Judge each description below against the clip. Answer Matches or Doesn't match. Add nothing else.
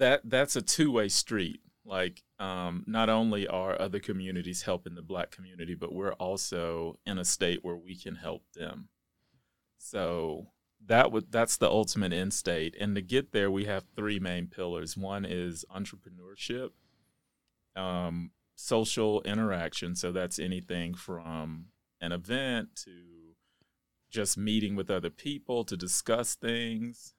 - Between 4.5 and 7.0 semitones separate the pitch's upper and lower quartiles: Doesn't match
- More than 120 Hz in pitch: Doesn't match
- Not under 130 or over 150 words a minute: Matches